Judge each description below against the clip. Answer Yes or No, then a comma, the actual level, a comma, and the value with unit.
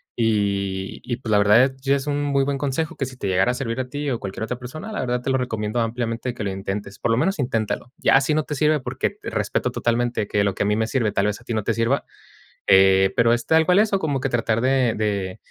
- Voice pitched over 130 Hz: No, low, 120 Hz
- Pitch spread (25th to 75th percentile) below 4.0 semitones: No, average, 4.4 semitones